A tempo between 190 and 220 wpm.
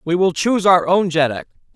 Yes: fast, 205 wpm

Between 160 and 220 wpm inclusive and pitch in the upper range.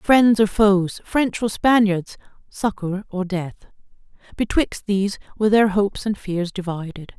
No: slow, 135 wpm; high, 200 Hz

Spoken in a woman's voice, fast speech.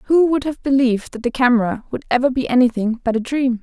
Yes: female; fast, 230 wpm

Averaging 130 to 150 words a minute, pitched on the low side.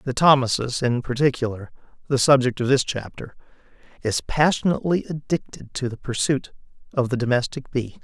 Yes: average, 140 wpm; low, 130 Hz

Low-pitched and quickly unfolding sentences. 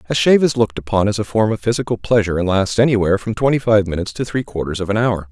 Yes: low, 105 Hz; fast, 270 wpm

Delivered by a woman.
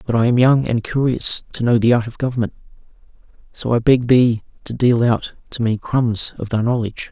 No: male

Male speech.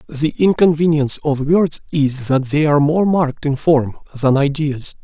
Yes: male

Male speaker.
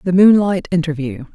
No: female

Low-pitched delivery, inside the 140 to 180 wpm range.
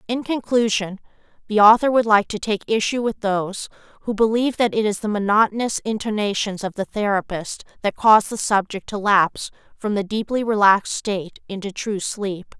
No: high, 210 Hz; average, 170 wpm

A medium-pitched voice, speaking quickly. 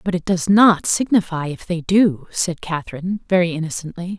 No: medium, 175 Hz; average, 170 wpm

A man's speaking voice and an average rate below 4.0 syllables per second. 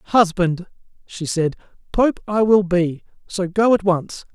Yes: male; 3.8 syllables/s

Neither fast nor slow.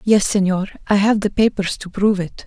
No: fast, 220 wpm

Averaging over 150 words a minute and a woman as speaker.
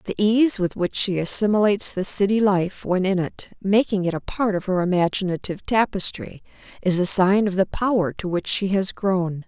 Yes: average, 195 wpm; female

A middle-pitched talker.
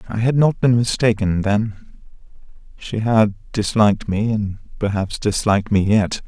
No: low, 105 Hz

